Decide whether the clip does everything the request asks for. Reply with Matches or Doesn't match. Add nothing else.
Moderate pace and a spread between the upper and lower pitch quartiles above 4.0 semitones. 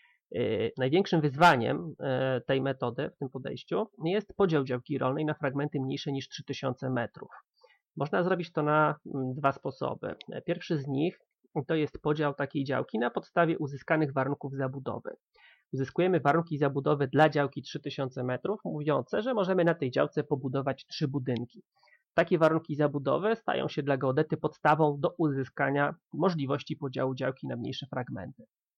Doesn't match